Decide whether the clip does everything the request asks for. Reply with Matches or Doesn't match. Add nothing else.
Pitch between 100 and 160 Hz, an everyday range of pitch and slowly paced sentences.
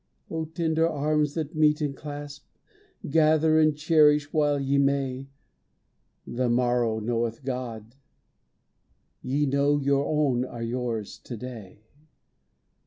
Matches